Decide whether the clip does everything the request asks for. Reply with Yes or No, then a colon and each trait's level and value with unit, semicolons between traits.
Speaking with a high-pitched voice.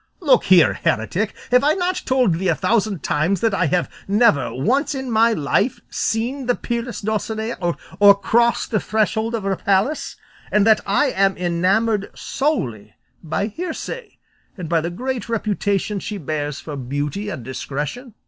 Yes: high, 205 Hz